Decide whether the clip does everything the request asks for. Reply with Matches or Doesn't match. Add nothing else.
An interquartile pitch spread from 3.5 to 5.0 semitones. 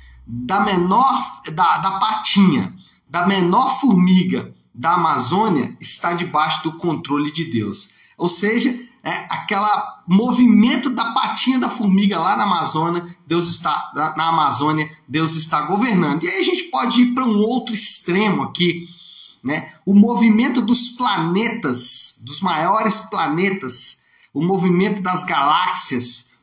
Doesn't match